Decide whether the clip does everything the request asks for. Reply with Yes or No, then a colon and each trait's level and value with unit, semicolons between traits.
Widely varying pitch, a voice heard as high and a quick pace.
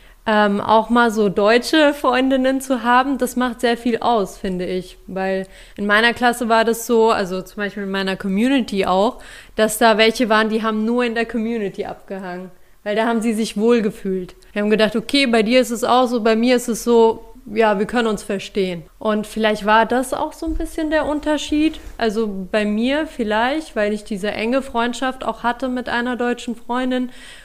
No: average, 2.9 semitones; high, 225 Hz; fast, 200 wpm